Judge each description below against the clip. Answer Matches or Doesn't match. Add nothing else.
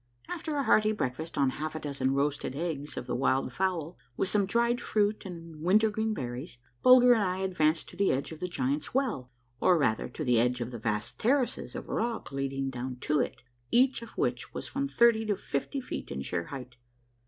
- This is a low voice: Doesn't match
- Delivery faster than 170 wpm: Matches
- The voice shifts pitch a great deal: Matches